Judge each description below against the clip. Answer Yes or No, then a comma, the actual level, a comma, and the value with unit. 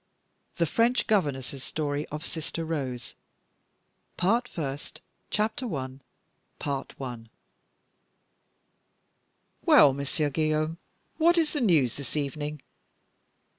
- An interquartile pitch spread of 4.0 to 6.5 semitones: Yes, average, 4.6 semitones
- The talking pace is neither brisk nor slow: No, slow, 90 wpm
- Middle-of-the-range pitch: Yes, medium, 150 Hz